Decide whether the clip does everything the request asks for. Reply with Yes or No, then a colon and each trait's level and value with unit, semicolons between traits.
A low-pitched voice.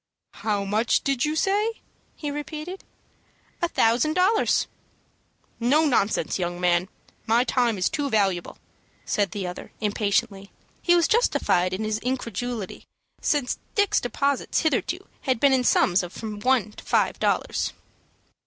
No: high, 240 Hz